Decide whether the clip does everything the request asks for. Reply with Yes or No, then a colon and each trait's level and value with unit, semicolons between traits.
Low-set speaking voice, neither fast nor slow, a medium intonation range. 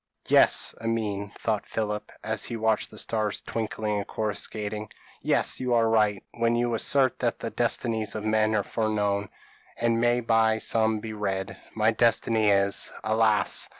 No: low, 110 Hz; average, 160 wpm; narrow, 1.4 semitones